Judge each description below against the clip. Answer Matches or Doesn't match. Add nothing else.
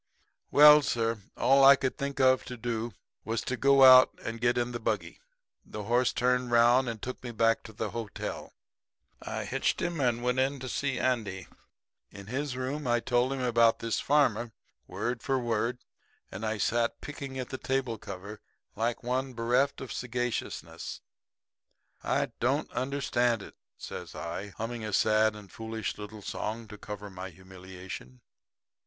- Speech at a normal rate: Matches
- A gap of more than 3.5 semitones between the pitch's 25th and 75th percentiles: Doesn't match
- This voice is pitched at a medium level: Doesn't match